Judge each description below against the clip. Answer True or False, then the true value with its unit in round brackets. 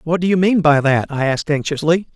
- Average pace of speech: False (250 wpm)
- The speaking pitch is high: False (160 Hz)